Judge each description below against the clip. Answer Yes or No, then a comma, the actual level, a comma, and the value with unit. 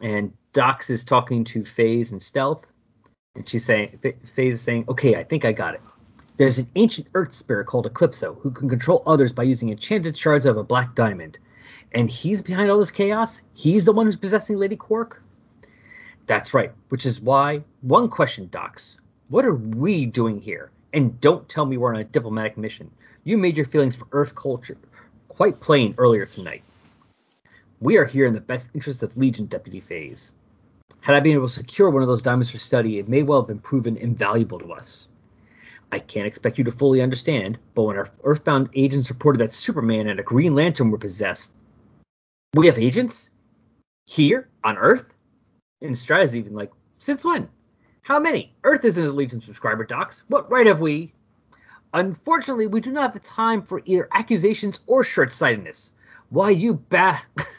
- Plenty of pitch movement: Yes, wide, 7.6 semitones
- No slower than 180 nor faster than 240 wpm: Yes, average, 185 wpm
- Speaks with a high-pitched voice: No, low, 135 Hz